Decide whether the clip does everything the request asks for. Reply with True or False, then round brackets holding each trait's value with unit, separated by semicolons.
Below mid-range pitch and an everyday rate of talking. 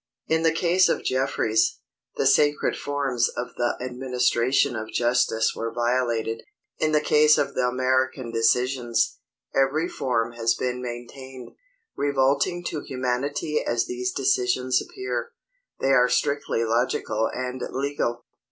False (125 Hz; 130 wpm)